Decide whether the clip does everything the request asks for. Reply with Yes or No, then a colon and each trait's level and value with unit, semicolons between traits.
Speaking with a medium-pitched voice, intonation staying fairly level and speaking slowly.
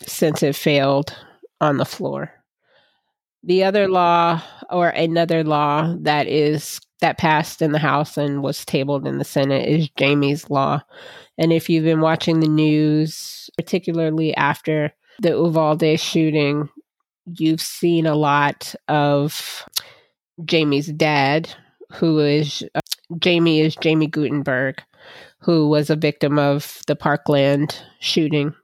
Yes: medium, 155 Hz; narrow, 2.0 semitones; slow, 130 wpm